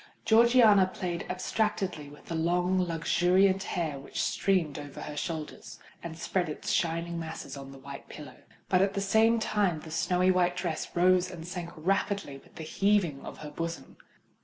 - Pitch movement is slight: No, average, 3.1 semitones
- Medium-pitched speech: Yes, medium, 175 Hz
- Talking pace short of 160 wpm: No, average, 170 wpm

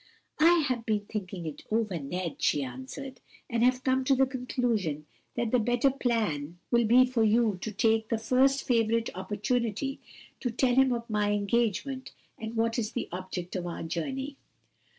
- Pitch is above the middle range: Yes, high, 230 Hz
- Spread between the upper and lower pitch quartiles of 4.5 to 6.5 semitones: No, average, 3.9 semitones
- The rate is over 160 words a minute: Yes, average, 170 wpm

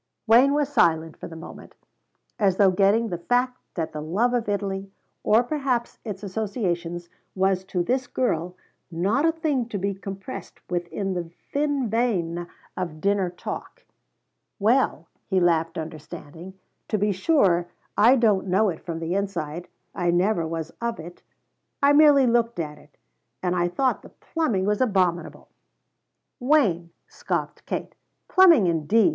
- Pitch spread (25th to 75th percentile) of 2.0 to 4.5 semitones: No, wide, 5.5 semitones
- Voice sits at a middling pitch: No, high, 195 Hz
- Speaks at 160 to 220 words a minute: No, average, 150 wpm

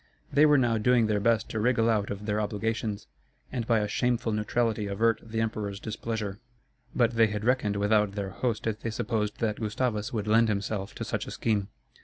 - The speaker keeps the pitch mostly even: Yes, narrow, 1.8 semitones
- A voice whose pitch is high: No, low, 110 Hz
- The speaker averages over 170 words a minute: Yes, average, 200 wpm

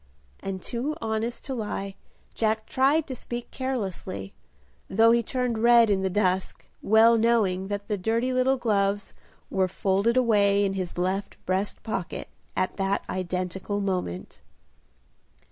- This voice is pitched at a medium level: No, high, 205 Hz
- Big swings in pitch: No, average, 3.6 semitones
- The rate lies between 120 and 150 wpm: Yes, average, 140 wpm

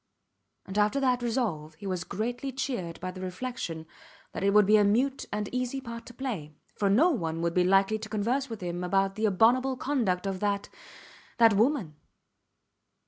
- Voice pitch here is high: Yes, high, 210 Hz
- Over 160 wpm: Yes, average, 185 wpm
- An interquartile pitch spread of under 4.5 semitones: No, average, 5.0 semitones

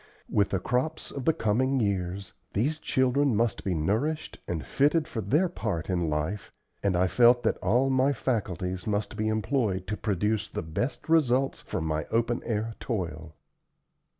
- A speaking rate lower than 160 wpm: No, average, 165 wpm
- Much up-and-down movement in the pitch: Yes, wide, 5.9 semitones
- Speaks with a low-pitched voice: Yes, low, 110 Hz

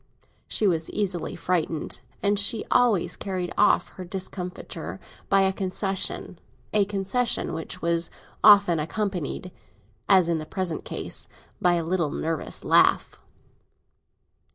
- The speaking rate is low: Yes, slow, 125 wpm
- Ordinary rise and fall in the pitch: Yes, average, 3.0 semitones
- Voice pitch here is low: No, medium, 185 Hz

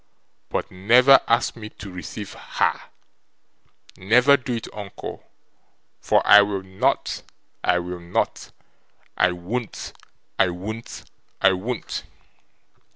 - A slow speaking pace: Yes, slow, 110 wpm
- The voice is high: No, low, 100 Hz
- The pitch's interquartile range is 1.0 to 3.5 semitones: No, average, 4.1 semitones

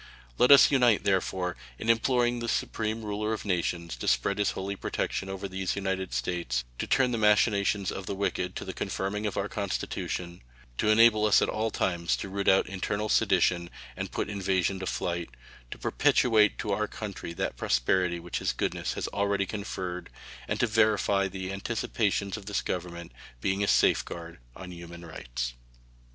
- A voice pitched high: No, low, 100 Hz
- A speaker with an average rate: Yes, average, 175 wpm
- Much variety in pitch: No, average, 3.0 semitones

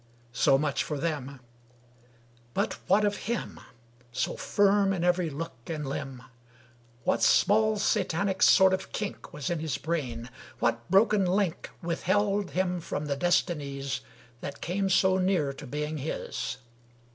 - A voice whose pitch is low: No, medium, 170 Hz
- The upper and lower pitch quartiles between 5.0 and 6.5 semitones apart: Yes, wide, 5.6 semitones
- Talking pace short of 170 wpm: Yes, average, 140 wpm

